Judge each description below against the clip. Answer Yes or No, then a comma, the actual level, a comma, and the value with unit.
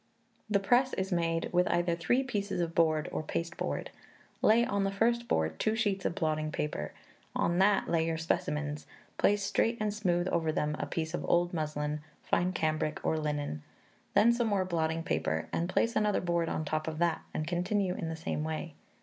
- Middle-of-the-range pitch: Yes, medium, 170 Hz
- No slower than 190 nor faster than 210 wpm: Yes, average, 195 wpm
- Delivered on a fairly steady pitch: No, average, 4.2 semitones